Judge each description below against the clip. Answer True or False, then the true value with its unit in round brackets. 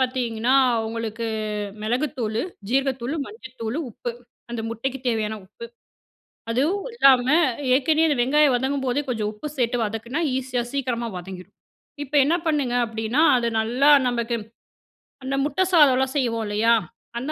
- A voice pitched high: True (250 Hz)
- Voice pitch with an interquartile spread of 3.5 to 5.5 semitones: False (3.1 semitones)